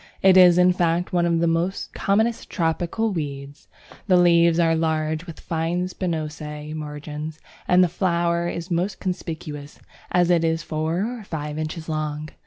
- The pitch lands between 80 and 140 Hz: No, medium, 165 Hz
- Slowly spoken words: No, average, 155 wpm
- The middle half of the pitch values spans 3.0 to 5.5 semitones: No, narrow, 2.4 semitones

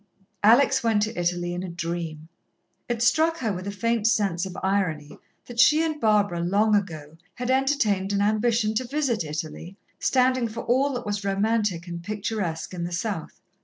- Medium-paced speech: Yes, average, 175 wpm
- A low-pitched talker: No, high, 205 Hz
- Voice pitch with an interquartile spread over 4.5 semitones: Yes, average, 5.1 semitones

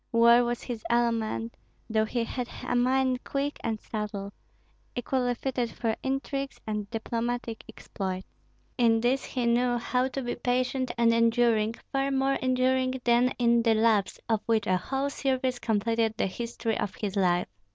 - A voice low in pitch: No, high, 235 Hz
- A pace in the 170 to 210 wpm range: No, average, 160 wpm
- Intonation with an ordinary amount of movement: No, narrow, 2.3 semitones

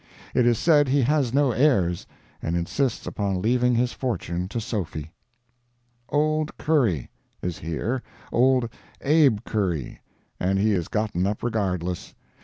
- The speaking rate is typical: No, slow, 130 wpm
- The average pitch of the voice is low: Yes, low, 110 Hz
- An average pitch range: No, wide, 6.4 semitones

